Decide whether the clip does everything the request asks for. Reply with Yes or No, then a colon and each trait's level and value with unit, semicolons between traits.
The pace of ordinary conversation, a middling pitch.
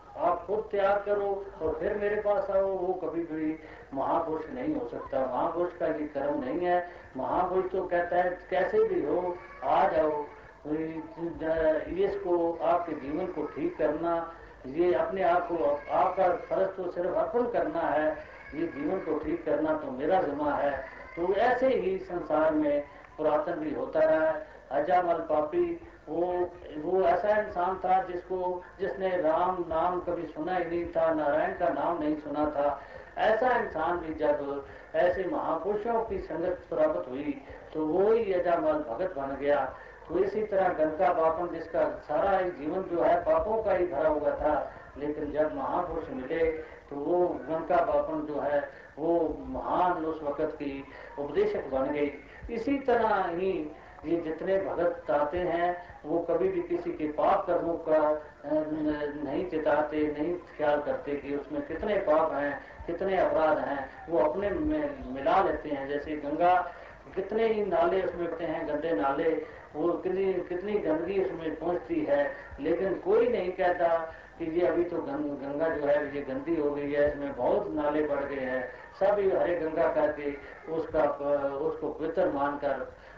Yes: average, 160 wpm; medium, 170 Hz